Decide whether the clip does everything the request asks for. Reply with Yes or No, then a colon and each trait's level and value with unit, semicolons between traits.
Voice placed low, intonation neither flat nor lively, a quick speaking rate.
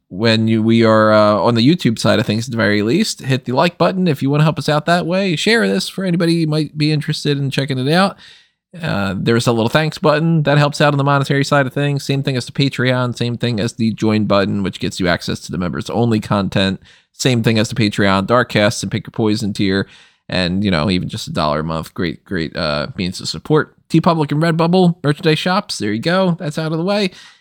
No: low, 130 Hz; wide, 6.1 semitones; fast, 250 wpm